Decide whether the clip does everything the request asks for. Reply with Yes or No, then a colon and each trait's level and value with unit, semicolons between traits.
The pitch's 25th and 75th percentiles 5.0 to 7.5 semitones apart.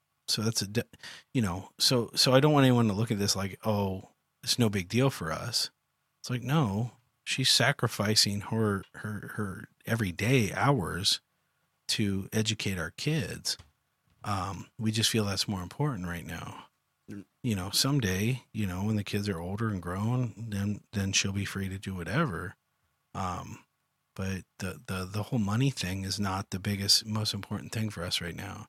No: average, 3.6 semitones